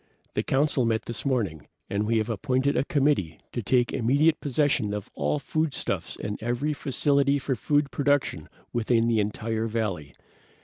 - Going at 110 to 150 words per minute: No, average, 160 wpm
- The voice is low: Yes, low, 120 Hz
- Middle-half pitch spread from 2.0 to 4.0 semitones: No, average, 4.5 semitones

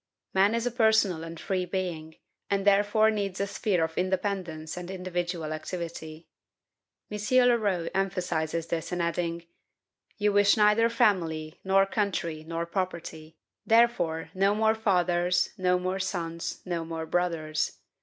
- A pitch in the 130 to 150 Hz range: No, medium, 180 Hz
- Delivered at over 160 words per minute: No, slow, 135 wpm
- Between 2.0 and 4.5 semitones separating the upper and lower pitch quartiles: Yes, average, 3.4 semitones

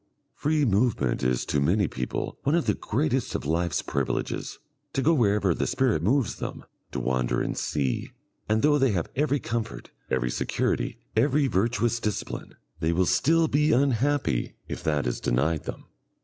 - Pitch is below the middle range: Yes, low, 110 Hz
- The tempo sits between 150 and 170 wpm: Yes, average, 165 wpm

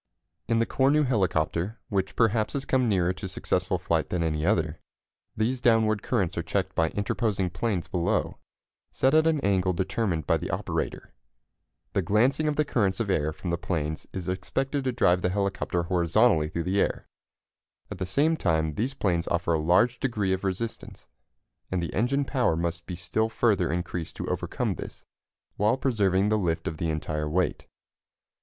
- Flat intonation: No, average, 5.1 semitones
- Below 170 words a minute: No, average, 175 wpm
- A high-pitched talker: No, very low, 95 Hz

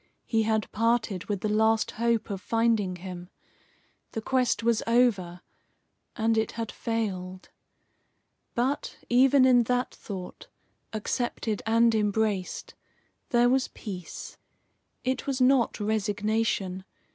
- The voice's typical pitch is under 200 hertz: No, high, 225 Hz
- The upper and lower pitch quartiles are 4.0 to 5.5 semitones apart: No, average, 2.8 semitones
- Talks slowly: Yes, slow, 115 wpm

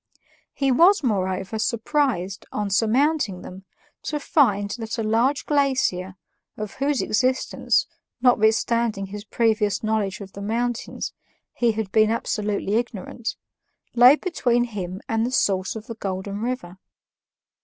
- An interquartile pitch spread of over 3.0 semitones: Yes, average, 3.6 semitones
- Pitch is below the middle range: No, high, 220 Hz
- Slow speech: Yes, slow, 130 wpm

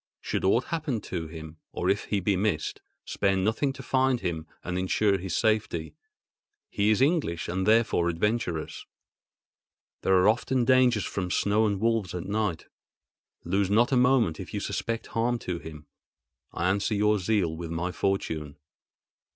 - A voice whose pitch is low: Yes, low, 100 Hz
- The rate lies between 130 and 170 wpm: Yes, average, 160 wpm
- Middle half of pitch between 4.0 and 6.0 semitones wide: Yes, average, 4.7 semitones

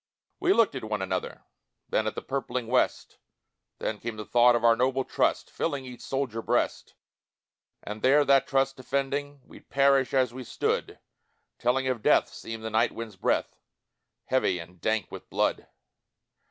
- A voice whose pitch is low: Yes, low, 125 Hz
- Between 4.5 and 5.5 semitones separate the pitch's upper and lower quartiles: No, average, 3.3 semitones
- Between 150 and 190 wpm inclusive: Yes, average, 165 wpm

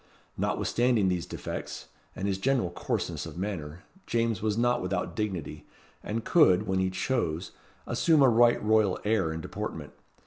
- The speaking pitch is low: Yes, low, 105 Hz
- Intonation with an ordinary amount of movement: Yes, average, 4.2 semitones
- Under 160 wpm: Yes, average, 150 wpm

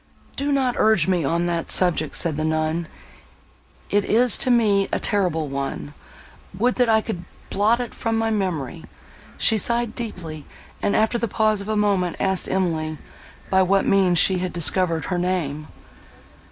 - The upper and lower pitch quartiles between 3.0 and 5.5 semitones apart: Yes, average, 4.9 semitones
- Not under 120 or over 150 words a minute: No, average, 165 wpm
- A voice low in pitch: No, high, 190 Hz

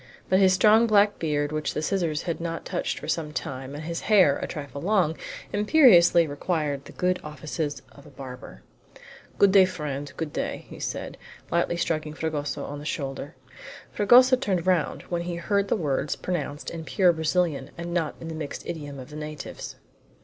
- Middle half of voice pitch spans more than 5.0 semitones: No, average, 3.8 semitones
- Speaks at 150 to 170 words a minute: No, average, 185 wpm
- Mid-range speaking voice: Yes, medium, 160 Hz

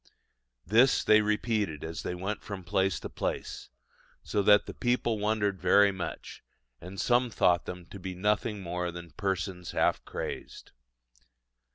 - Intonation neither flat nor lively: Yes, average, 3.0 semitones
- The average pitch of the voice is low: Yes, low, 100 Hz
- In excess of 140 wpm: Yes, average, 150 wpm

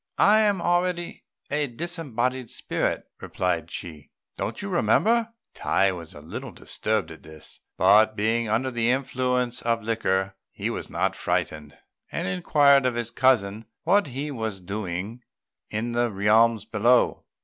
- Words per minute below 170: Yes, average, 145 wpm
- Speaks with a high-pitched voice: No, low, 115 Hz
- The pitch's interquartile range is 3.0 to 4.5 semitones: No, average, 4.9 semitones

